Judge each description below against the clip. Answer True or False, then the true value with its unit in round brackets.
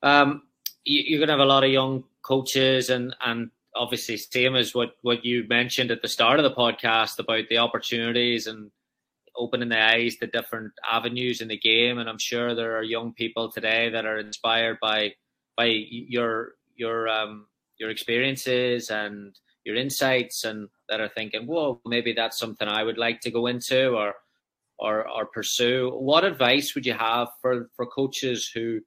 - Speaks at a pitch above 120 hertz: False (115 Hz)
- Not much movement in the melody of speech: True (1.9 semitones)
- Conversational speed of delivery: True (180 wpm)